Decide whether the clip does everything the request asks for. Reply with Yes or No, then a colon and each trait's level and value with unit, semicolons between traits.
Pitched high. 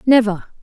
Yes: high, 220 Hz